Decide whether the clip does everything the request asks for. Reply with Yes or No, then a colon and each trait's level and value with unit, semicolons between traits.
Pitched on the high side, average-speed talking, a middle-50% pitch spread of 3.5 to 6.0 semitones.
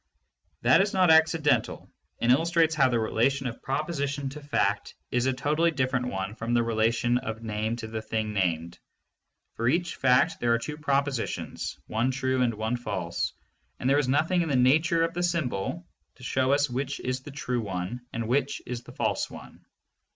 No: low, 130 Hz; average, 190 wpm; average, 4.2 semitones